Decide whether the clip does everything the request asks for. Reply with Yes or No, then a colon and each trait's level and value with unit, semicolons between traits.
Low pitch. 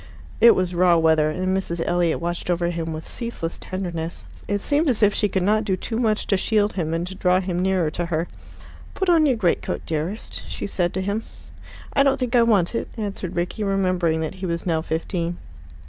No: medium, 185 Hz